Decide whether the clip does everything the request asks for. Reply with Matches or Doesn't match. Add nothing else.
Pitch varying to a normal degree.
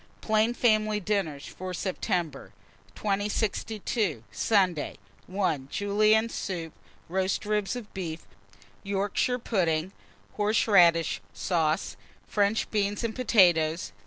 Matches